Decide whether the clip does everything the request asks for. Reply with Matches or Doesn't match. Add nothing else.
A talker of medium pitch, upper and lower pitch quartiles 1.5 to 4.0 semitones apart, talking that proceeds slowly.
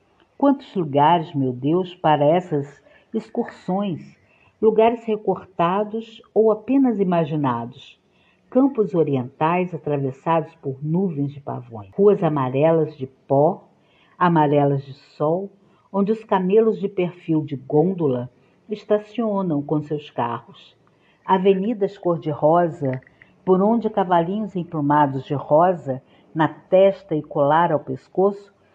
Doesn't match